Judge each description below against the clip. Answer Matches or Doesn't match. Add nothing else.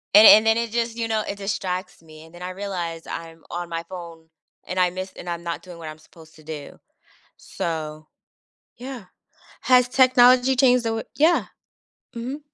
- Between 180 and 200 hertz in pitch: Matches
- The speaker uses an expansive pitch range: Matches